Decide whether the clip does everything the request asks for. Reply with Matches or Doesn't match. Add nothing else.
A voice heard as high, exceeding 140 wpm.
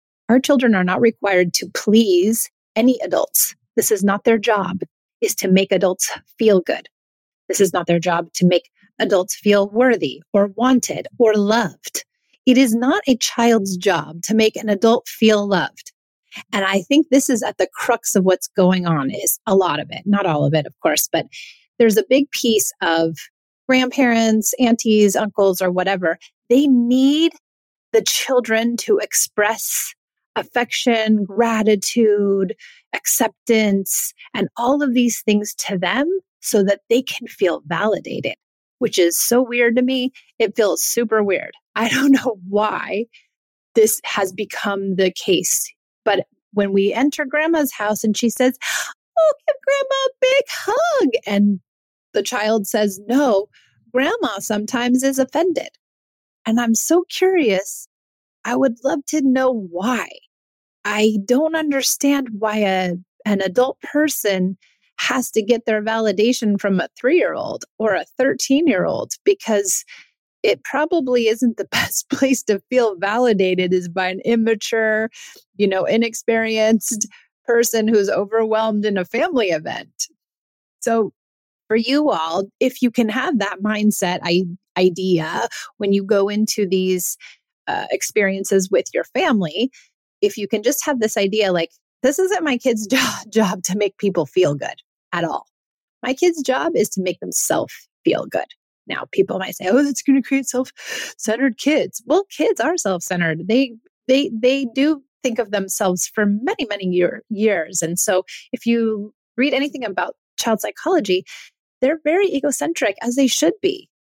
Matches